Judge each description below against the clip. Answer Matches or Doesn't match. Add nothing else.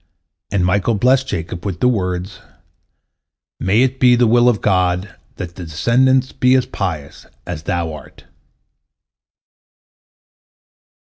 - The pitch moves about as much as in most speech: Doesn't match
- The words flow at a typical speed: Doesn't match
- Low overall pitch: Matches